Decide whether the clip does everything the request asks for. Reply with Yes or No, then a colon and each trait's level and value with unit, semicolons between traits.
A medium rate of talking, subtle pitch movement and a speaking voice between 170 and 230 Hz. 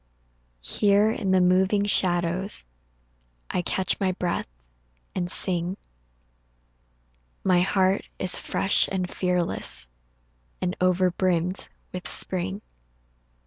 No: slow, 100 wpm; narrow, 1.3 semitones; medium, 185 Hz